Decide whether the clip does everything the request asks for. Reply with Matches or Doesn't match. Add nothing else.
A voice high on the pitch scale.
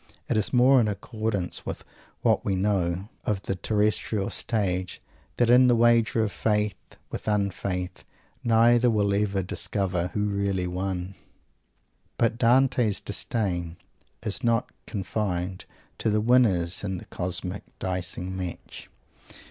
Doesn't match